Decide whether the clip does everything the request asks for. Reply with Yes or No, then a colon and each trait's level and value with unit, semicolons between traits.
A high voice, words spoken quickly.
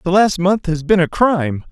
No: medium, 175 Hz; fast, 245 wpm